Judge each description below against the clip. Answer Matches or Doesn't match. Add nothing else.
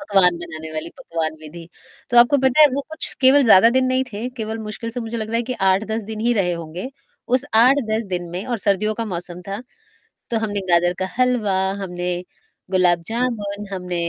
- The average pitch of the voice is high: Matches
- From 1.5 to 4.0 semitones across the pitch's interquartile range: Doesn't match